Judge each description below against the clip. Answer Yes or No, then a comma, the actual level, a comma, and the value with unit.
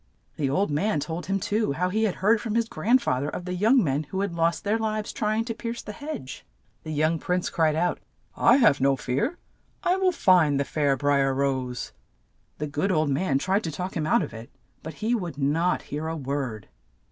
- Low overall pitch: No, medium, 170 Hz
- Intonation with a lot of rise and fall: Yes, wide, 6.8 semitones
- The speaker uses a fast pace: Yes, fast, 230 wpm